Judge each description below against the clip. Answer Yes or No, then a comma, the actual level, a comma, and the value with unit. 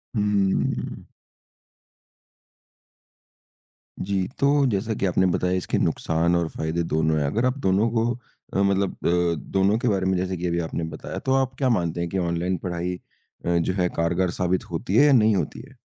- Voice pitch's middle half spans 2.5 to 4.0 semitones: Yes, average, 3.3 semitones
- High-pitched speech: No, very low, 95 Hz